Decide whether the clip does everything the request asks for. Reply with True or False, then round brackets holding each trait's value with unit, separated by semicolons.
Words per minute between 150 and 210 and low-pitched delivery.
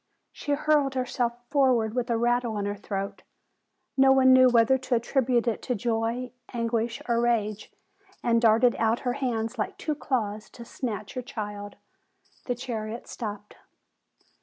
False (160 wpm; 235 Hz)